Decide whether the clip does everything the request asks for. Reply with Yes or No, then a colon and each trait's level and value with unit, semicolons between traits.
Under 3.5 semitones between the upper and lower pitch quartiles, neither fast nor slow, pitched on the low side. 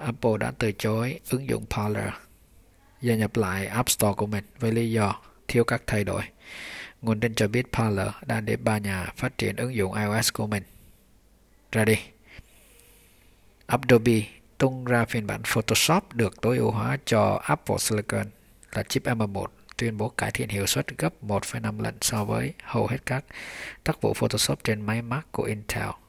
Yes: average, 2.7 semitones; average, 175 wpm; low, 110 Hz